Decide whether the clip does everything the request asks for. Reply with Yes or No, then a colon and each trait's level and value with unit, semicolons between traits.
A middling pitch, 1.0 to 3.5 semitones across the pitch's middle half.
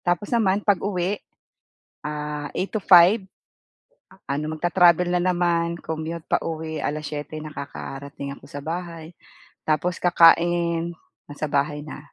Yes: medium, 165 Hz; average, 2.8 semitones